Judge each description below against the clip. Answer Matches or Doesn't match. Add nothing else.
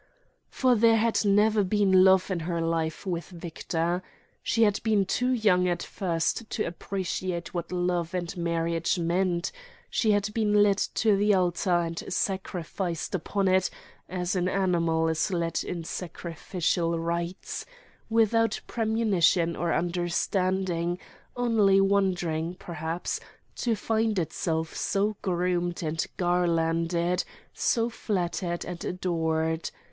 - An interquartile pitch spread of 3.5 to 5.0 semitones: Doesn't match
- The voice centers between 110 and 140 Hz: Doesn't match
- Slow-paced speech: Matches